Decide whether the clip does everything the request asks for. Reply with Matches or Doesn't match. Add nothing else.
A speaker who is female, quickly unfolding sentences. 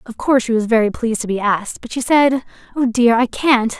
Matches